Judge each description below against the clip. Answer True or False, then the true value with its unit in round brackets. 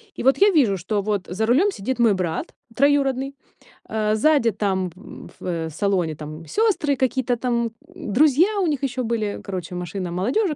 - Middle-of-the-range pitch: False (230 Hz)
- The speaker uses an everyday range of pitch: False (6.7 semitones)